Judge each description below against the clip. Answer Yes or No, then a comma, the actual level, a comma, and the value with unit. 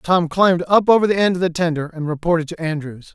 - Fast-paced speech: Yes, fast, 250 wpm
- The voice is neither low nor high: Yes, medium, 170 Hz